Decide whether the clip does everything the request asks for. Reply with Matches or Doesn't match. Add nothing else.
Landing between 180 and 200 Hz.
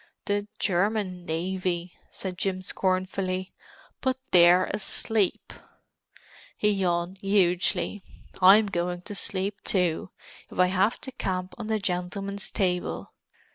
Matches